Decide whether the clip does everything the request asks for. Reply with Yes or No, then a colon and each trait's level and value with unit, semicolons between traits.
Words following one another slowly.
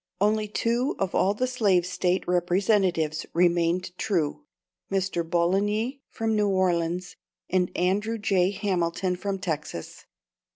Yes: slow, 120 wpm